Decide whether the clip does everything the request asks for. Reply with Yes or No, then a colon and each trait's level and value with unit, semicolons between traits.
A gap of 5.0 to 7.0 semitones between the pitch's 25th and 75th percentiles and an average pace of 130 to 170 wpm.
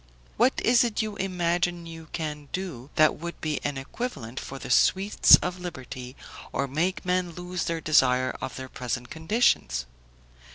Yes: wide, 5.5 semitones; average, 160 wpm